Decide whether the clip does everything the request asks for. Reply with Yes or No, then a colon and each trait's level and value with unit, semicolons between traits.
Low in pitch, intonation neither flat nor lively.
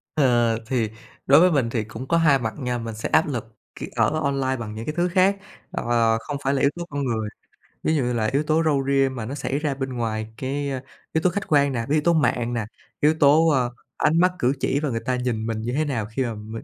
Yes: low, 130 Hz; average, 4.3 semitones